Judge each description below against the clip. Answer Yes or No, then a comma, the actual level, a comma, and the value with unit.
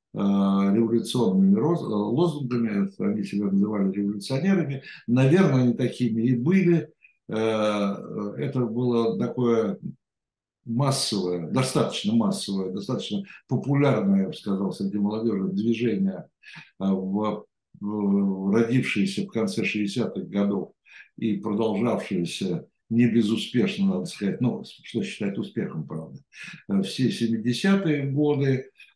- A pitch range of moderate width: No, wide, 5.9 semitones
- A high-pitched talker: No, low, 115 Hz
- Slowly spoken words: Yes, slow, 95 wpm